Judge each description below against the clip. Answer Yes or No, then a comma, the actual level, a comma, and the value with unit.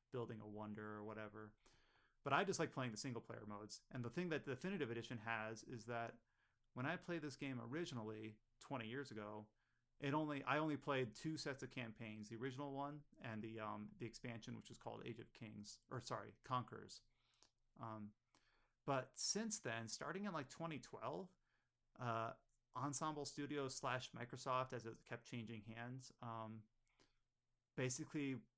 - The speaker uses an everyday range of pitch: Yes, average, 3.9 semitones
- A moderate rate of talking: Yes, average, 165 wpm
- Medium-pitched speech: No, low, 120 Hz